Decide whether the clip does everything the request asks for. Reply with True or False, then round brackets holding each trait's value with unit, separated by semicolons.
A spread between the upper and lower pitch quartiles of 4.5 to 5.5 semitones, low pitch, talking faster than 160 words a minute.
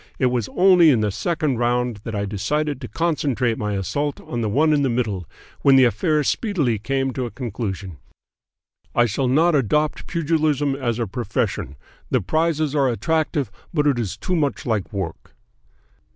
True (5.1 semitones; 130 Hz; 175 wpm)